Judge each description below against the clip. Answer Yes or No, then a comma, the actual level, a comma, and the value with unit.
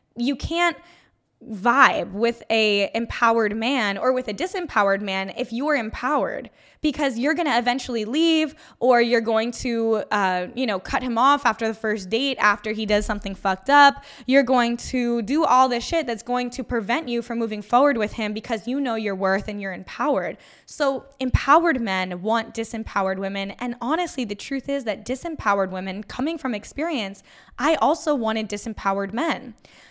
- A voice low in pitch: No, high, 235 Hz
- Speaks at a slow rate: No, average, 175 wpm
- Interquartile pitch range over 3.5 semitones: Yes, average, 4.4 semitones